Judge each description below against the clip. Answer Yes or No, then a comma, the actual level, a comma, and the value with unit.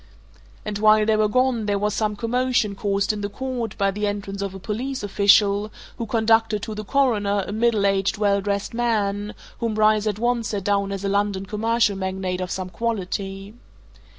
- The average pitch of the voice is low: No, high, 210 Hz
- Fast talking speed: No, average, 190 wpm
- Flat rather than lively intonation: Yes, narrow, 2.1 semitones